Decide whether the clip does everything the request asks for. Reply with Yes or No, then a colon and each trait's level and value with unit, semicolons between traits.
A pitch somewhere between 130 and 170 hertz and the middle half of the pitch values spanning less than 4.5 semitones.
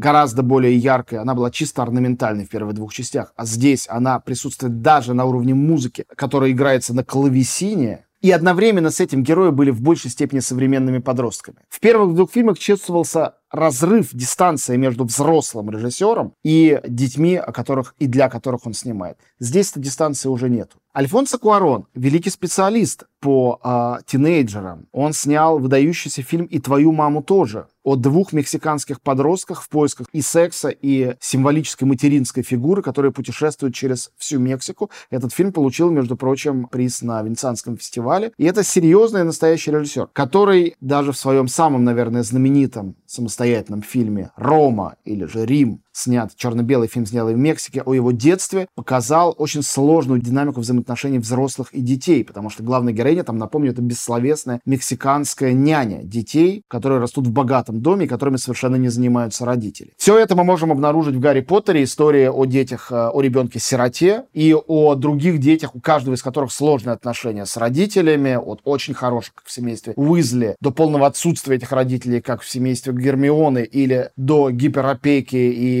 Yes: low, 135 Hz; average, 3.8 semitones